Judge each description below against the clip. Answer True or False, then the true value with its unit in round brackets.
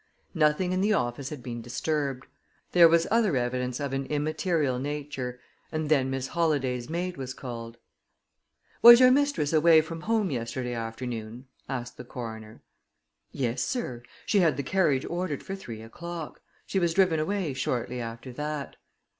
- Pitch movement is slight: False (5.4 semitones)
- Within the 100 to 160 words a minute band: True (155 wpm)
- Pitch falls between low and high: True (145 Hz)